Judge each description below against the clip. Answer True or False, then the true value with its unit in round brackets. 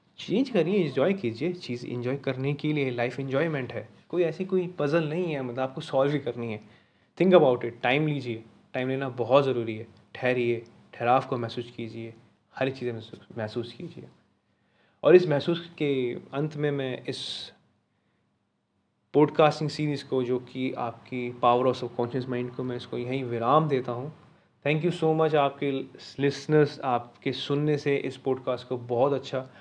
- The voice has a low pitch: True (130 Hz)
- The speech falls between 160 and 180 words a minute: True (170 wpm)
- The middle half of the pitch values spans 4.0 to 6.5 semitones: False (3.5 semitones)